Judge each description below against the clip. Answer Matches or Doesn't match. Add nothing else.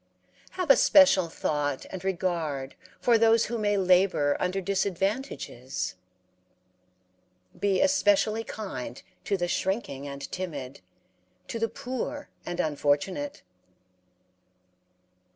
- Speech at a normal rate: Doesn't match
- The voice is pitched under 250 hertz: Matches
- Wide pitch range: Matches